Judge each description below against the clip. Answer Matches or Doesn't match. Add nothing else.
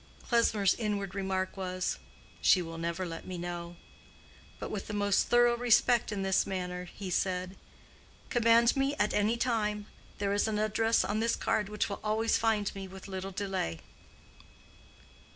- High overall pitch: Matches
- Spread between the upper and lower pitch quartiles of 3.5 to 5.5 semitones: Doesn't match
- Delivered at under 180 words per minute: Matches